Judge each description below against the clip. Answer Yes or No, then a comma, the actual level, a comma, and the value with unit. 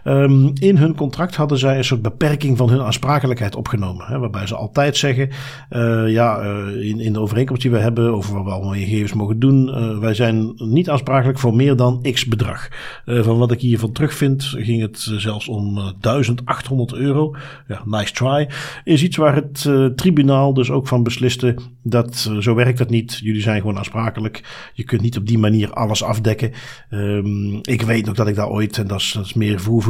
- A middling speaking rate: No, fast, 215 wpm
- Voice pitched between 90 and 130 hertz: Yes, low, 120 Hz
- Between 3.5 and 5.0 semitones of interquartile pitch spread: Yes, average, 3.8 semitones